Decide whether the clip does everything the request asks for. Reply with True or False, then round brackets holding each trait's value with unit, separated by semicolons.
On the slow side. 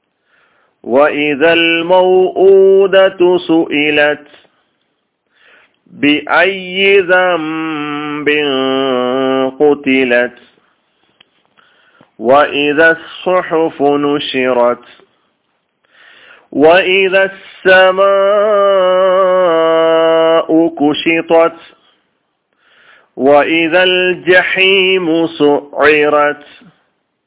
True (35 wpm)